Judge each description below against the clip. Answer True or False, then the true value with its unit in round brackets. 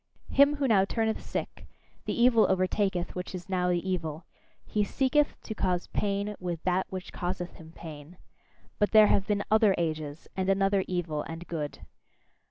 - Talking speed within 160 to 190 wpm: True (170 wpm)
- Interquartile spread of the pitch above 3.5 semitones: False (3.2 semitones)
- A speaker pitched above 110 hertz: True (185 Hz)